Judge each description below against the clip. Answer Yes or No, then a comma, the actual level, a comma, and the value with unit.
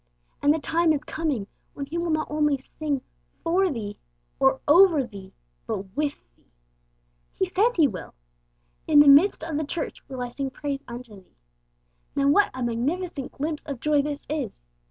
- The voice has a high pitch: Yes, very high, 290 Hz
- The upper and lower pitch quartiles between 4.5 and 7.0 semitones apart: No, average, 3.5 semitones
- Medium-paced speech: Yes, average, 175 wpm